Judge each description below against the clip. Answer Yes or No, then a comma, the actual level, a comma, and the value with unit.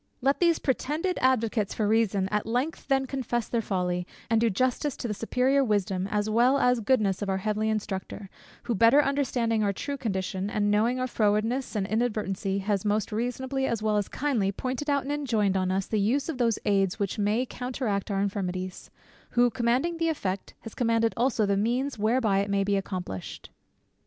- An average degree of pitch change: Yes, average, 4.1 semitones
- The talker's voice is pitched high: Yes, high, 220 Hz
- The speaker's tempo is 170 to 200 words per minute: Yes, average, 190 wpm